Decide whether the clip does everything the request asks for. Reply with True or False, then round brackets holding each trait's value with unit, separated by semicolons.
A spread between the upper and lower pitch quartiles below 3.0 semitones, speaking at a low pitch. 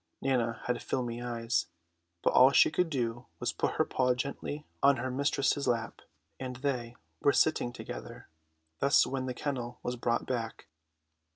True (2.4 semitones; 125 Hz)